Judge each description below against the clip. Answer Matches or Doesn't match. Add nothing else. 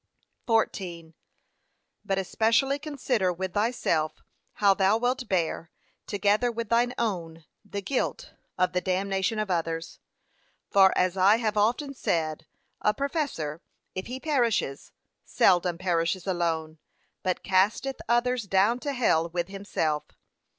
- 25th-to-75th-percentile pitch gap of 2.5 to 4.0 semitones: Doesn't match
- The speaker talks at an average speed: Doesn't match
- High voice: Matches